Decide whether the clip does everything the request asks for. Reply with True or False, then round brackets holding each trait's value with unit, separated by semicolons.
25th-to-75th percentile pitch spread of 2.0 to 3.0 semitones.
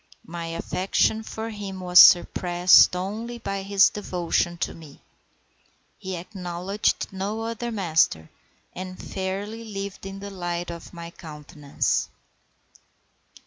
True (2.7 semitones)